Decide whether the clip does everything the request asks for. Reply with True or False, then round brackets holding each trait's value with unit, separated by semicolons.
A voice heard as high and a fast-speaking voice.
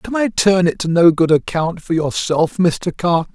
False (175 Hz; 215 wpm)